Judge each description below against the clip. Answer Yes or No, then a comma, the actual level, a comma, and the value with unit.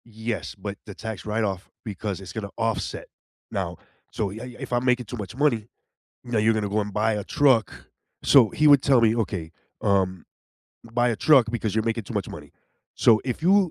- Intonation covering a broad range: No, average, 2.9 semitones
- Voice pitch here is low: Yes, low, 110 Hz